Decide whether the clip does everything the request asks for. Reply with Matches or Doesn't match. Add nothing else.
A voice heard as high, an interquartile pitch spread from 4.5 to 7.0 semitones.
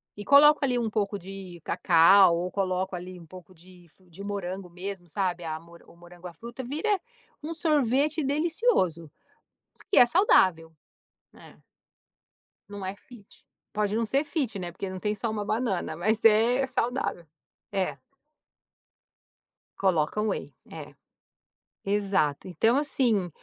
Matches